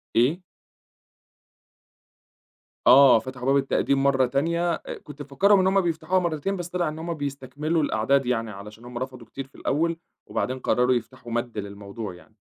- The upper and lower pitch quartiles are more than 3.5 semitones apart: Yes, average, 5.0 semitones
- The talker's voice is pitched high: No, low, 135 Hz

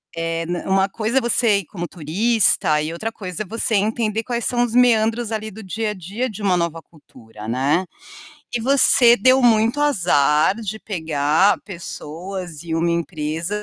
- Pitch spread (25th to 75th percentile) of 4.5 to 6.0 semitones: Yes, average, 5.3 semitones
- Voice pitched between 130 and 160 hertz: No, high, 195 Hz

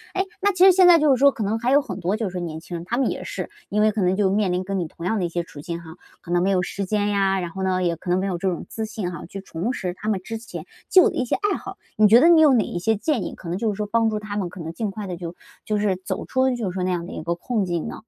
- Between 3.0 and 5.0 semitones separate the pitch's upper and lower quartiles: Yes, average, 4.3 semitones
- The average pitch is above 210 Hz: No, high, 200 Hz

